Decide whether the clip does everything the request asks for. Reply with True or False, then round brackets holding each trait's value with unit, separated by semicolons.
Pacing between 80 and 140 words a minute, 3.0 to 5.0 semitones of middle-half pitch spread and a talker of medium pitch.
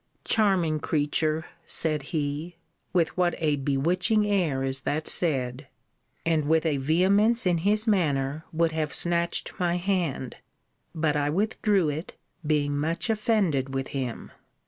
True (135 wpm; 3.9 semitones; 160 Hz)